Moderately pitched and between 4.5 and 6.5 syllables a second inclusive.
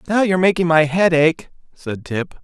Yes: medium, 165 Hz; 5.0 syllables/s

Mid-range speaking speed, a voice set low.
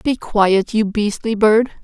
No: average, 165 wpm; high, 215 Hz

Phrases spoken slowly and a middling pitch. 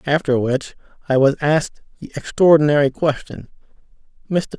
Yes: slow, 120 wpm; medium, 145 Hz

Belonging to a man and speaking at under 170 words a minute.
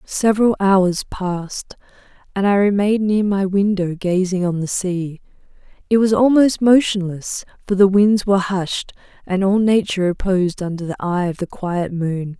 No: female; average, 160 wpm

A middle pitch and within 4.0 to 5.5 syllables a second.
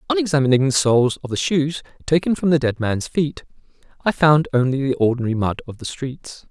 No: medium, 145 Hz; 5.7 syllables/s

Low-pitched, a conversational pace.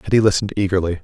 Yes: low, 100 Hz; average, 175 wpm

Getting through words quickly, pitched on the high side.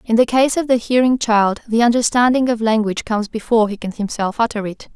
Yes: fast, 220 wpm; high, 225 Hz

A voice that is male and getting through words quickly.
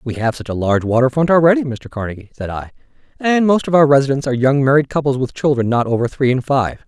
Yes: male; fast, 245 wpm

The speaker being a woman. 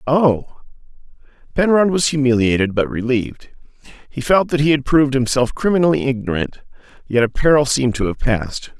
No: male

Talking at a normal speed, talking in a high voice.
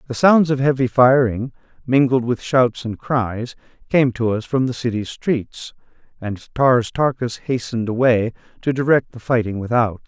No: average, 160 wpm; low, 125 Hz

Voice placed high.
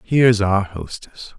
No: low, 105 Hz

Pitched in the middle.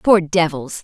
Yes: medium, 165 Hz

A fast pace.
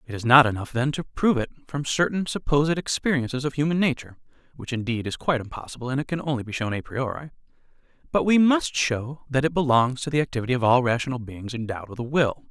Yes: fast, 220 wpm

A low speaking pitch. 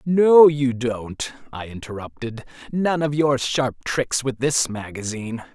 Yes: low, 130 Hz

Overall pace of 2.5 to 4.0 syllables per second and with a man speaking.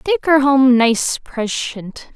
No: 3.1 syllables/s; female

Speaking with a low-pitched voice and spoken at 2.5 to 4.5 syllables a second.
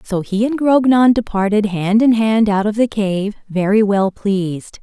No: high, 210 Hz; 4.3 syllables/s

